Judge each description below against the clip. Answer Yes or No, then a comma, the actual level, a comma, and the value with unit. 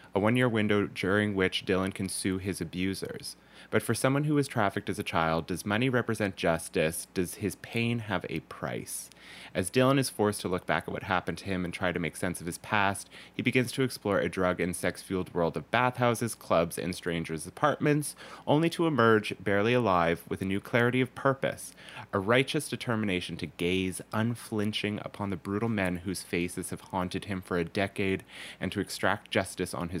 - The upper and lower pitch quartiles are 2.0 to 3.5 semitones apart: No, average, 4.5 semitones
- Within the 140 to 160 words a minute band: No, average, 200 wpm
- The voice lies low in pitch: Yes, low, 100 Hz